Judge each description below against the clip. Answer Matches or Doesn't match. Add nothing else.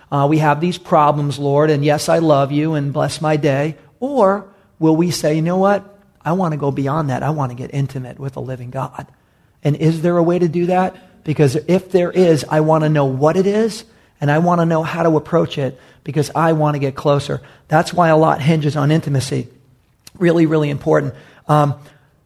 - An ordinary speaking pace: Doesn't match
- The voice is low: Doesn't match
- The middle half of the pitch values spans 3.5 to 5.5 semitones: Doesn't match